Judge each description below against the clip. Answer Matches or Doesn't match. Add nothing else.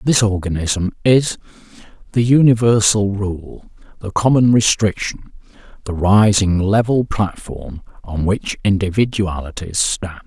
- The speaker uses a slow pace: Matches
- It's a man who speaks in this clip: Matches